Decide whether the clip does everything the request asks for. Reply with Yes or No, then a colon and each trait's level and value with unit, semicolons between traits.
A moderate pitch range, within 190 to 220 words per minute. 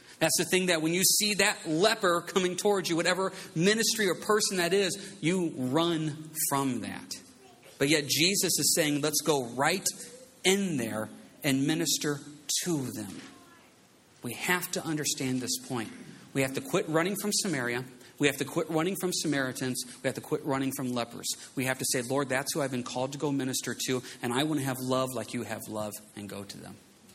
No: wide, 5.7 semitones; average, 200 wpm